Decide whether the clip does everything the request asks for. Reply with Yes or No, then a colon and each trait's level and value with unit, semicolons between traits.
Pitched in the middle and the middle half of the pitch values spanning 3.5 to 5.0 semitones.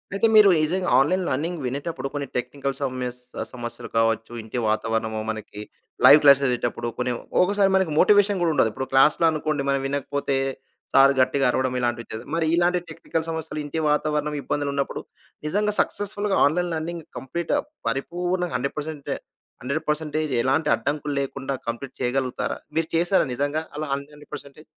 Yes: medium, 145 Hz; average, 3.9 semitones